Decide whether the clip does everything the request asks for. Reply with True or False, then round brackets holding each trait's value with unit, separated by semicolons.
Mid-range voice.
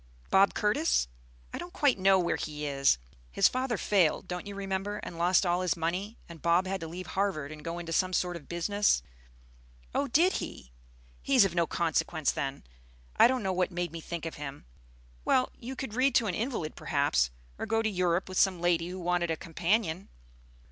True (180 Hz)